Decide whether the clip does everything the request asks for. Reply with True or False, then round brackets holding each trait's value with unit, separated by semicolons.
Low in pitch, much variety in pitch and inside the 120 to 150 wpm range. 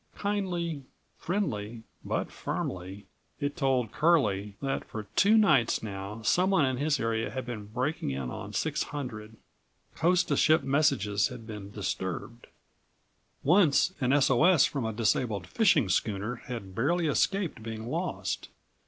True (125 Hz; 6.8 semitones; 140 wpm)